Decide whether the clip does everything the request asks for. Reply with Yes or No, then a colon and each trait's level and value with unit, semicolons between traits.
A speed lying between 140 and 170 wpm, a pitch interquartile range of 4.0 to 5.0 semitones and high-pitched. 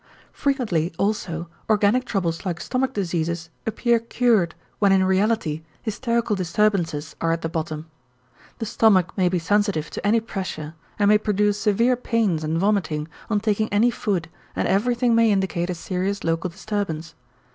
Yes: average, 155 wpm; average, 4.5 semitones; high, 200 Hz